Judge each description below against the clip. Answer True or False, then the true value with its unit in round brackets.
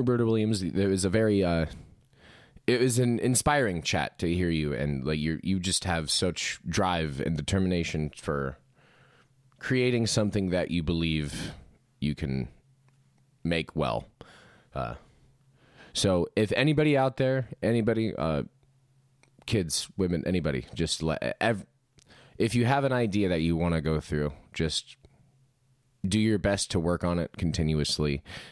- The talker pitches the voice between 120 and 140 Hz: False (95 Hz)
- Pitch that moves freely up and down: True (7.8 semitones)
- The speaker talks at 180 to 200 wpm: False (145 wpm)